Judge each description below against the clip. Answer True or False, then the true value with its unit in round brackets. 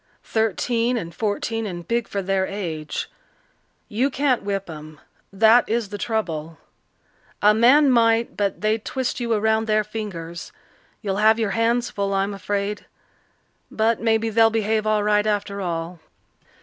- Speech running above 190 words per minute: False (150 wpm)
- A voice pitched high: True (215 Hz)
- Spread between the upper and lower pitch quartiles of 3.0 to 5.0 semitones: False (2.4 semitones)